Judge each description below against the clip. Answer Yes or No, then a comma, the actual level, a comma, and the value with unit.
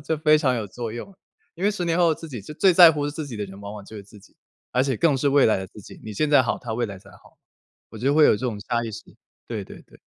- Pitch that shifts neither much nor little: No, wide, 6.0 semitones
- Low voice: Yes, low, 130 Hz